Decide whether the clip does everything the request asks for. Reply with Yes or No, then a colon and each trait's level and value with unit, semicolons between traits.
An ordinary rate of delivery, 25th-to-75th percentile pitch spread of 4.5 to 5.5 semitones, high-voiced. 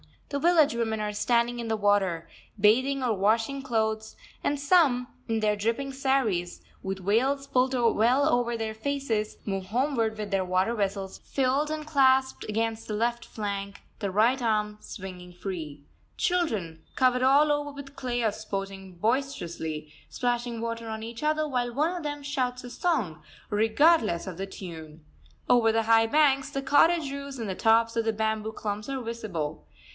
Yes: average, 170 wpm; average, 4.8 semitones; high, 230 Hz